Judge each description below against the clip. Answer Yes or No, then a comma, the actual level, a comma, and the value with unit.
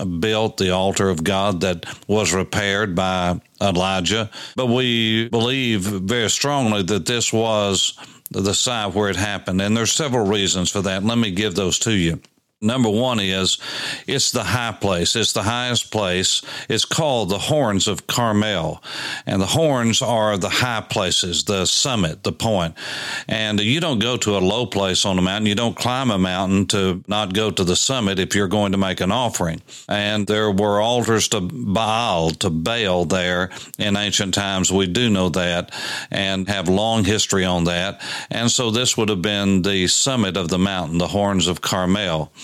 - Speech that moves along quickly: No, average, 180 wpm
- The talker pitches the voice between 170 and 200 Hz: No, low, 100 Hz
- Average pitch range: Yes, average, 3.0 semitones